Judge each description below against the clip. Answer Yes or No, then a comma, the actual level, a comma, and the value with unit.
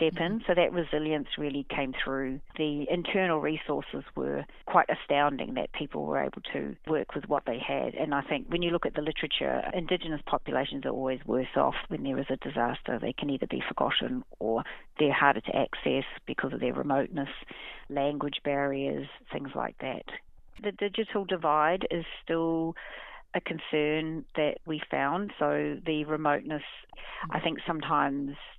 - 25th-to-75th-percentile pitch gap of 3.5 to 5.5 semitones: No, average, 3.0 semitones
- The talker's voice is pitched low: No, medium, 150 Hz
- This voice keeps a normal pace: Yes, average, 165 wpm